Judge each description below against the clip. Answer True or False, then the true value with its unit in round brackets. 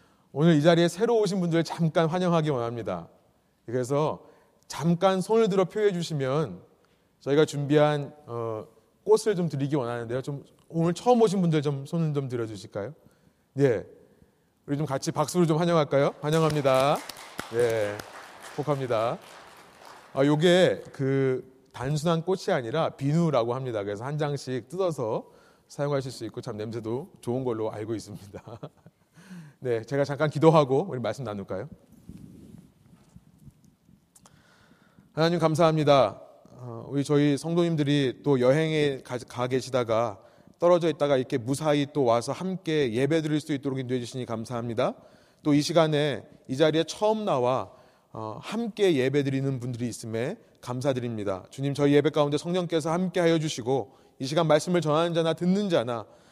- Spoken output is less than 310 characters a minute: False (315 characters per minute)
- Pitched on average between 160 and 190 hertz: False (145 Hz)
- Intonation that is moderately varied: True (4.5 semitones)